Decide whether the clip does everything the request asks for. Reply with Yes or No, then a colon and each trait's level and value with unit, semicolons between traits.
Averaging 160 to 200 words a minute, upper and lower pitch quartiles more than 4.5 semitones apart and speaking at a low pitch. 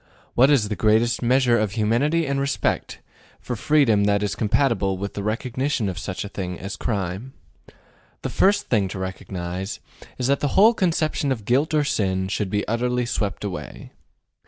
Yes: average, 175 wpm; wide, 5.5 semitones; low, 110 Hz